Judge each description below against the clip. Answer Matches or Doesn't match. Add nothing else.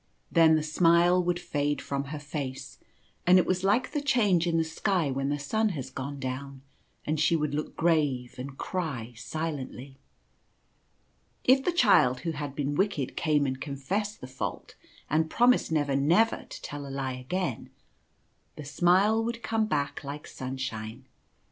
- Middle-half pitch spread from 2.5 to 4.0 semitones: Doesn't match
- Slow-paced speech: Doesn't match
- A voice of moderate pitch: Matches